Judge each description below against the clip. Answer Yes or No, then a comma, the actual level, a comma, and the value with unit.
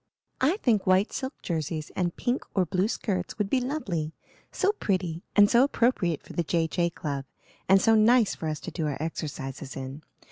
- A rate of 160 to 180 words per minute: No, average, 190 wpm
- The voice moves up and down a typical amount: No, wide, 6.0 semitones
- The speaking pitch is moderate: Yes, medium, 180 Hz